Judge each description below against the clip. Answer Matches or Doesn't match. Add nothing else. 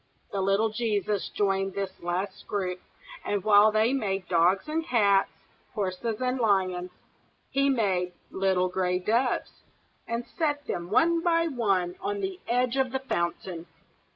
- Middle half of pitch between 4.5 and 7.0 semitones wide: Matches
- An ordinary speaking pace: Matches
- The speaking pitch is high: Matches